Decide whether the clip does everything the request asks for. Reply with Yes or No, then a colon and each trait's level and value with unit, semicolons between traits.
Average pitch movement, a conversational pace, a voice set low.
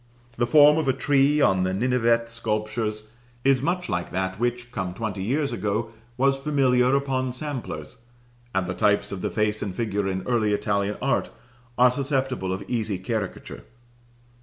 Yes: average, 4.6 semitones; average, 160 wpm; low, 115 Hz